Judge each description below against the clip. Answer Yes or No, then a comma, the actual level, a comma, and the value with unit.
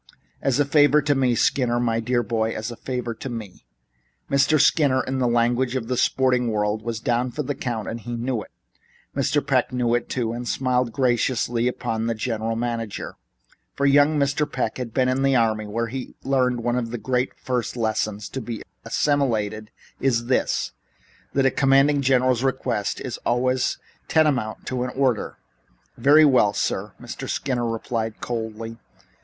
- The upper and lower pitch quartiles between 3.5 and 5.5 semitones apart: No, narrow, 2.6 semitones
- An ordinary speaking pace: Yes, average, 170 wpm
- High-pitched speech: No, low, 125 Hz